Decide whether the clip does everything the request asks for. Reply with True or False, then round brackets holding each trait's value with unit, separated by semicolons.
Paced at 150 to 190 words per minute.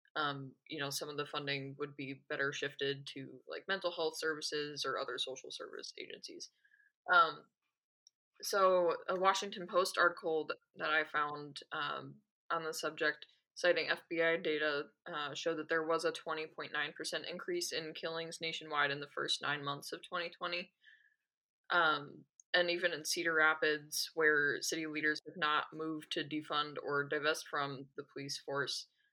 True (155 wpm)